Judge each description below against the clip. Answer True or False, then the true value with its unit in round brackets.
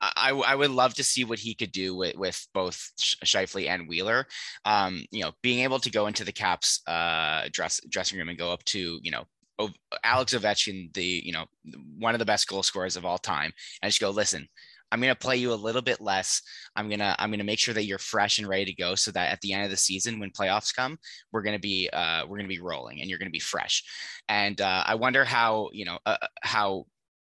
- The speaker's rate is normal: False (245 wpm)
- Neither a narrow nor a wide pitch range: True (3.7 semitones)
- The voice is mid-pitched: False (105 Hz)